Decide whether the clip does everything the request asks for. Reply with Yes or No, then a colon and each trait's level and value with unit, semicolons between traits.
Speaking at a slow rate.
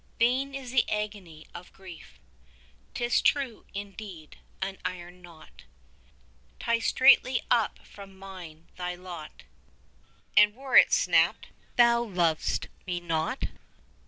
Yes: slow, 120 wpm